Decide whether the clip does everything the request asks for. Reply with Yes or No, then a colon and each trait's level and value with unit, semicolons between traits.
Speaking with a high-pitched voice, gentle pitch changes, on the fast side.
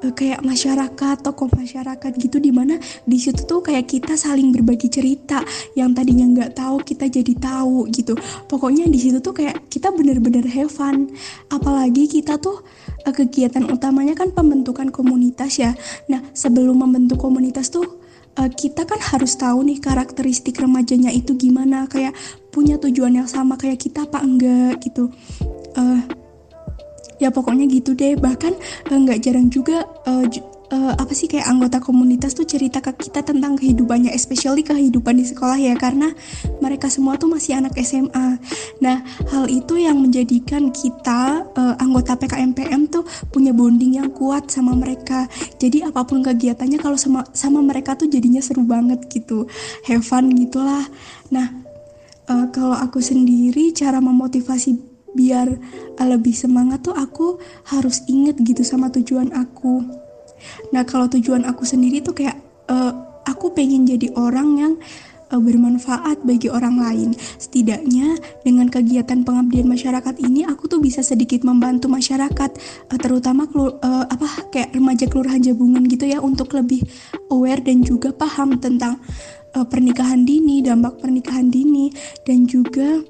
Yes: very high, 260 Hz; narrow, 1.8 semitones; fast, 145 wpm